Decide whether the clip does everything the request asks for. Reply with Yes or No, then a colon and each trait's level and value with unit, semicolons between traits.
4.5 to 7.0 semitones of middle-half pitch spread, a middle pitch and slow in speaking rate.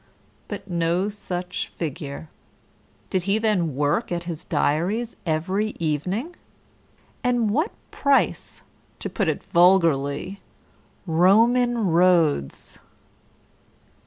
Yes: average, 4.8 semitones; medium, 180 Hz; slow, 95 wpm